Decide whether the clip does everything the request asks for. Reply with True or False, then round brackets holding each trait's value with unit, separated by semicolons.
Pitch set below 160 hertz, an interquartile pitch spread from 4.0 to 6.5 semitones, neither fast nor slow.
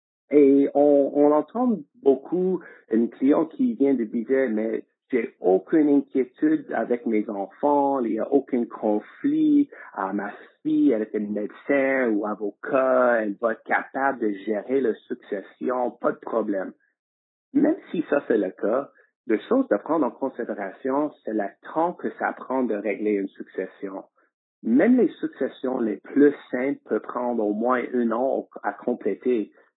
True (135 Hz; 5.0 semitones; 160 wpm)